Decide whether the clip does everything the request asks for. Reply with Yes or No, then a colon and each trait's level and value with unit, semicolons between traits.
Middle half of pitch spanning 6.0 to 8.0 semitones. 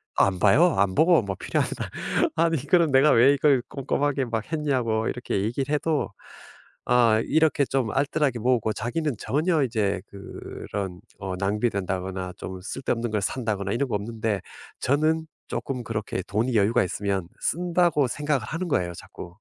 Yes: wide, 6.3 semitones